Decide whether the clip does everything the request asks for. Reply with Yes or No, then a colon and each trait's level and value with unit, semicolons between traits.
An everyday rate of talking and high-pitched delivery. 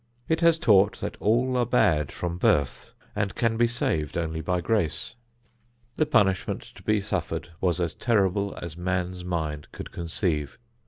No: average, 160 wpm; very low, 95 Hz